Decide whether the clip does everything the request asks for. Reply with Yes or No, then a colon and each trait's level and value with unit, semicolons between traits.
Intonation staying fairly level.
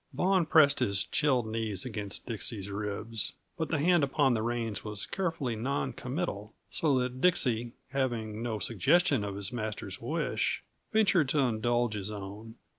No: average, 4.9 semitones